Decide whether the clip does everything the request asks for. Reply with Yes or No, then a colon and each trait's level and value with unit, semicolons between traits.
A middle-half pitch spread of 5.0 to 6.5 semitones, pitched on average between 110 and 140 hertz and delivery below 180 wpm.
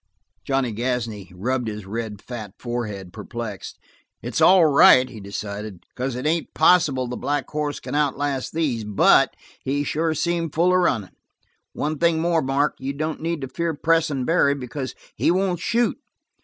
Yes: wide, 5.4 semitones; low, 135 Hz; average, 165 wpm